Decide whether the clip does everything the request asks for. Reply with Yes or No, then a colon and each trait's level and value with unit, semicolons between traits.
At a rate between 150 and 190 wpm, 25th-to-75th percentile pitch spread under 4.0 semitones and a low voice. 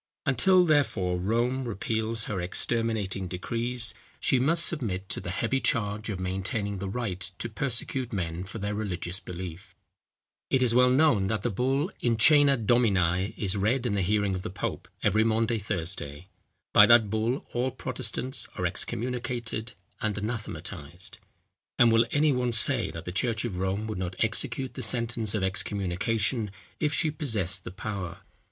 No: average, 160 wpm; average, 4.3 semitones; low, 110 Hz